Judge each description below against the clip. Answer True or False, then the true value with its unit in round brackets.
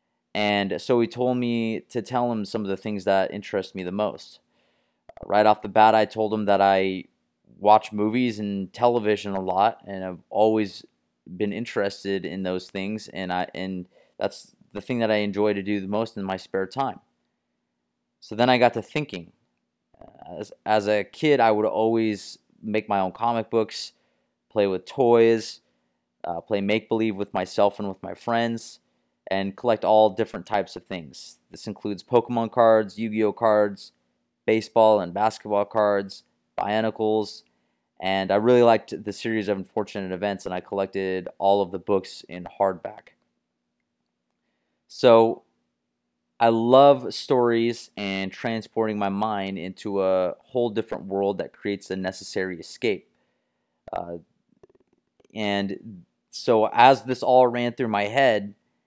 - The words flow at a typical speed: True (155 wpm)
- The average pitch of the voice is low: True (105 Hz)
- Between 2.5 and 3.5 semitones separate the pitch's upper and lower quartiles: True (3.0 semitones)